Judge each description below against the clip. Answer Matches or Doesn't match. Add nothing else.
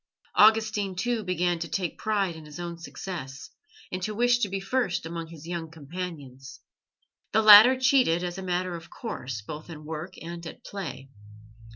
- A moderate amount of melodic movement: Matches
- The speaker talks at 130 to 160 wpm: Doesn't match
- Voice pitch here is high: Doesn't match